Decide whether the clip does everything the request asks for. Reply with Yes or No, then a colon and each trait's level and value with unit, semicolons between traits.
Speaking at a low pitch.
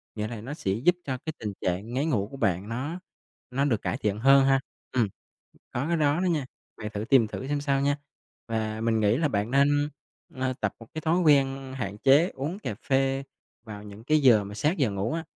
Yes: low, 130 Hz